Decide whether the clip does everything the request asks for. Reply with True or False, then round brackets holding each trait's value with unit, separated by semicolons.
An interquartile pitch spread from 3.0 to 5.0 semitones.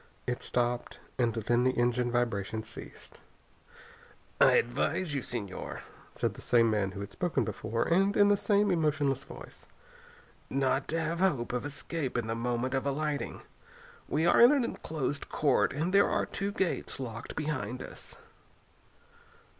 False (5.4 semitones)